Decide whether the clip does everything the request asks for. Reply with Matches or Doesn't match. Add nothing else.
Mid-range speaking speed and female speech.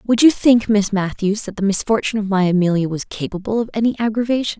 Doesn't match